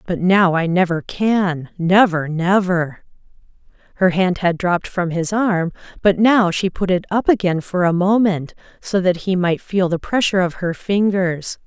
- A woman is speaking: Yes, female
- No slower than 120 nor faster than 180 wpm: Yes, average, 170 wpm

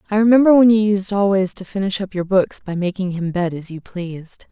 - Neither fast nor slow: No, fast, 240 wpm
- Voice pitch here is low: No, high, 190 Hz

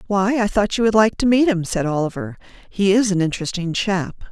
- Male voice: No, female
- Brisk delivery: Yes, fast, 220 wpm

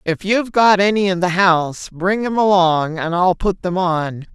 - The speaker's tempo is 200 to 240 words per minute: Yes, fast, 205 wpm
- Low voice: No, medium, 185 Hz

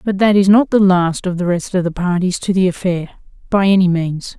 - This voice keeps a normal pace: No, fast, 245 wpm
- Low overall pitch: No, medium, 185 Hz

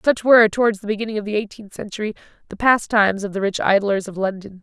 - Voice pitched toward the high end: Yes, high, 210 Hz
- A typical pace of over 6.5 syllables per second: Yes, 6.7 syllables/s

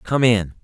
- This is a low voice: Yes, low, 110 Hz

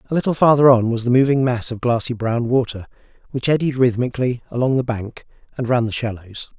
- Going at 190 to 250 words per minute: Yes, average, 200 wpm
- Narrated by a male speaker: Yes, male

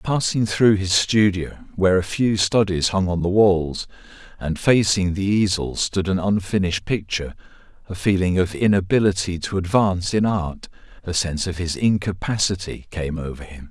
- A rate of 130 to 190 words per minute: Yes, average, 160 wpm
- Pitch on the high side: No, very low, 95 Hz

